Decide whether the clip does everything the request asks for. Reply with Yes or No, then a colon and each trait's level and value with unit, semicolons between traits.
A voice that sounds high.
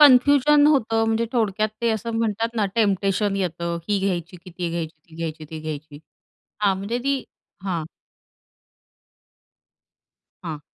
Yes: high, 200 Hz